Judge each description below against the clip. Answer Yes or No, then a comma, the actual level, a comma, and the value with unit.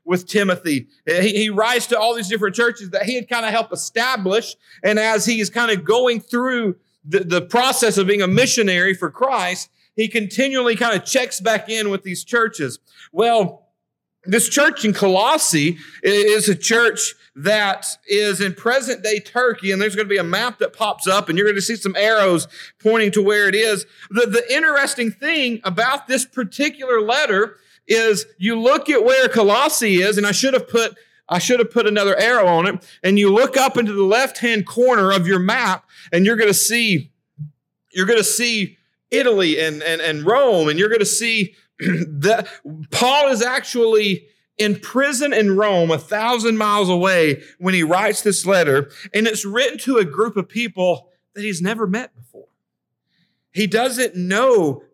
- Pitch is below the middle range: No, high, 210 Hz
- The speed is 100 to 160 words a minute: No, average, 180 wpm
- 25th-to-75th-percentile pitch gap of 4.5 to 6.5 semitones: No, average, 3.7 semitones